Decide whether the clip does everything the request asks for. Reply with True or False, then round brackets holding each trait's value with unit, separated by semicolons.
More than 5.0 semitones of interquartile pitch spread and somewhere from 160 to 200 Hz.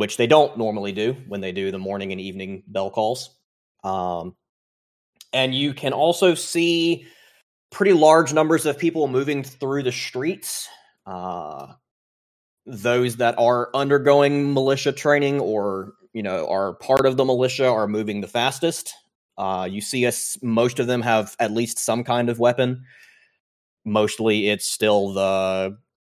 False (5.5 semitones; 120 Hz)